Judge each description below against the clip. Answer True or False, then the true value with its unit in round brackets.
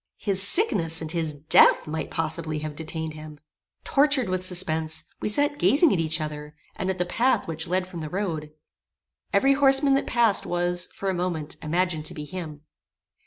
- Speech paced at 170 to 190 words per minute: True (180 wpm)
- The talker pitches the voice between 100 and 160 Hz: False (175 Hz)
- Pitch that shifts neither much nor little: True (4.0 semitones)